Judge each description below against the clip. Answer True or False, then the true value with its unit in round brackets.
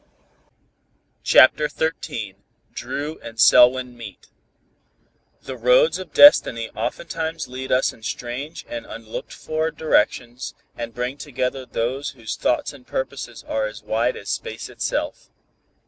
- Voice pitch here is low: True (130 Hz)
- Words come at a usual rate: False (125 wpm)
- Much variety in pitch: False (4.4 semitones)